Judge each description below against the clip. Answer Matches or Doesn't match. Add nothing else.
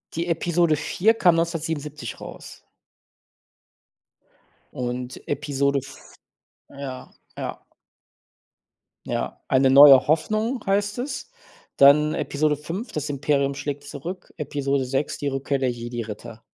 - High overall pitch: Doesn't match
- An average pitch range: Matches